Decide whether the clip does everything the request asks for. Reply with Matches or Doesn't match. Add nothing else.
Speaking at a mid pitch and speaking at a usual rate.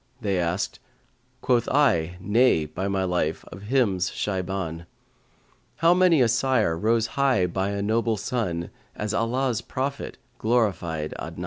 Doesn't match